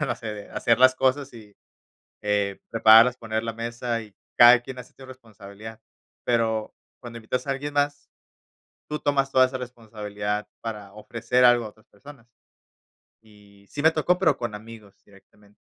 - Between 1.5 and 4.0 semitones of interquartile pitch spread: Yes, average, 3.4 semitones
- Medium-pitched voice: No, low, 115 Hz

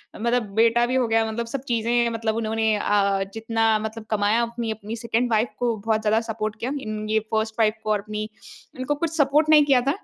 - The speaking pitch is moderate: No, high, 225 Hz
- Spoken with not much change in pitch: Yes, narrow, 1.7 semitones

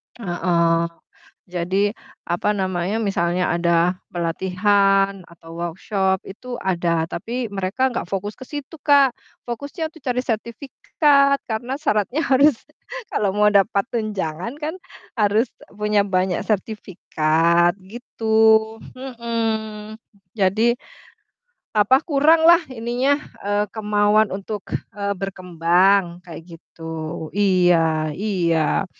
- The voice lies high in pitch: Yes, high, 205 Hz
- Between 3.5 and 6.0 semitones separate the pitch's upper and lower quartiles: Yes, average, 4.7 semitones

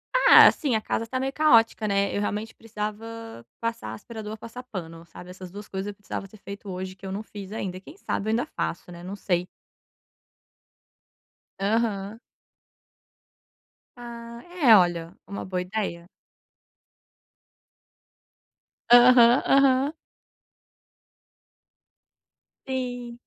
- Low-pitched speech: No, high, 215 Hz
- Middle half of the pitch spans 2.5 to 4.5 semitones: Yes, average, 3.8 semitones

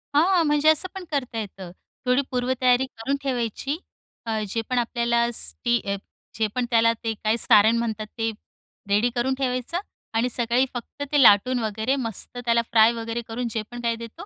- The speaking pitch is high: Yes, high, 235 Hz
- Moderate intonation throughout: No, narrow, 2.2 semitones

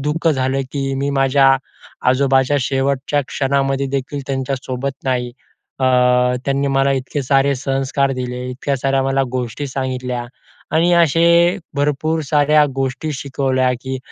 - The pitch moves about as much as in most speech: No, narrow, 1.2 semitones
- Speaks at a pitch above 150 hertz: No, low, 135 Hz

